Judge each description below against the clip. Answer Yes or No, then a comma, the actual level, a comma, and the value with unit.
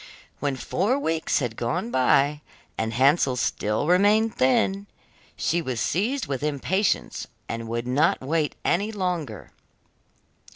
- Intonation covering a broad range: Yes, wide, 6.8 semitones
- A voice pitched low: No, medium, 145 Hz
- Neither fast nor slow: No, slow, 125 wpm